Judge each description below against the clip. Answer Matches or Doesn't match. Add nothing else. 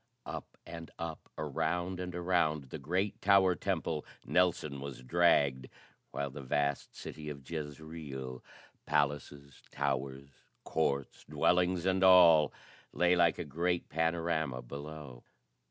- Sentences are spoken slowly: Matches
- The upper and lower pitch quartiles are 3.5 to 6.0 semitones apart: Matches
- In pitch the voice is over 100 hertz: Doesn't match